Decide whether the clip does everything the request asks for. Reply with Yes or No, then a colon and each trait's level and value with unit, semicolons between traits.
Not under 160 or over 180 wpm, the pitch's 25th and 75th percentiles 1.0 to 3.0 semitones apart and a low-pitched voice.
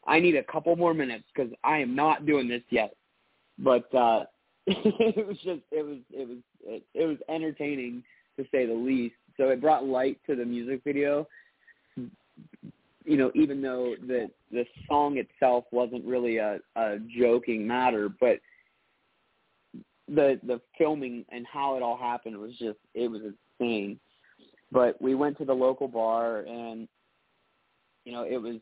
No: average, 165 wpm; average, 3.4 semitones; low, 125 Hz